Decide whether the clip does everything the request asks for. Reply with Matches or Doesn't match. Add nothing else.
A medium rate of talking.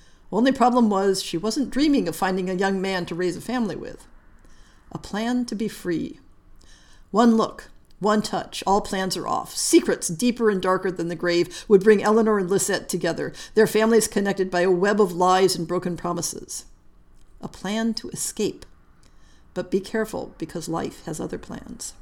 Matches